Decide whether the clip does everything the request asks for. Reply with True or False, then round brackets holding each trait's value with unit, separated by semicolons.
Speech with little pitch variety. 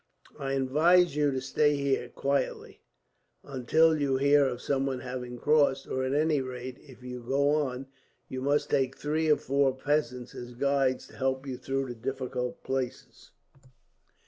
True (1.8 semitones)